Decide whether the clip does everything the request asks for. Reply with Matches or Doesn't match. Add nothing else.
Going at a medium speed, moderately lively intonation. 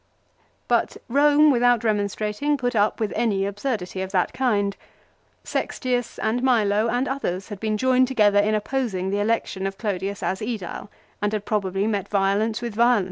Matches